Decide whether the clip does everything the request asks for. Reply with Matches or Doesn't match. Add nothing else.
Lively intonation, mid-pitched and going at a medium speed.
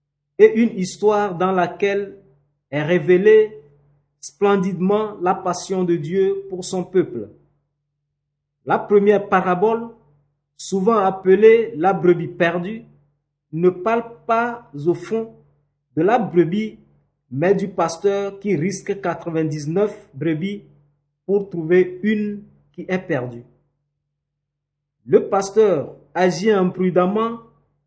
Doesn't match